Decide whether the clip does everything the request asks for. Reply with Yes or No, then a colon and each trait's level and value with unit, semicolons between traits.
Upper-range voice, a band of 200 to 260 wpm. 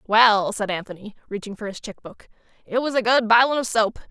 Yes: high, 220 Hz; fast, 205 wpm